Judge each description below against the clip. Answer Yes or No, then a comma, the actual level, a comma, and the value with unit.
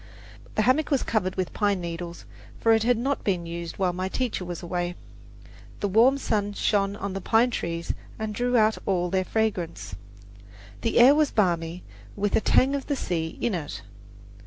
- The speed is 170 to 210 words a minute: Yes, average, 180 wpm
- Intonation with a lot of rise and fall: No, average, 4.6 semitones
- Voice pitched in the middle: No, high, 200 Hz